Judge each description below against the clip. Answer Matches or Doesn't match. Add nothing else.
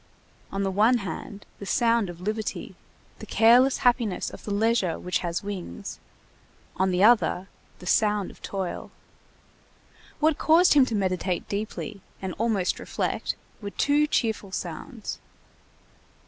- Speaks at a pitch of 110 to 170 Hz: Doesn't match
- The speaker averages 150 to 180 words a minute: Doesn't match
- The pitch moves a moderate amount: Matches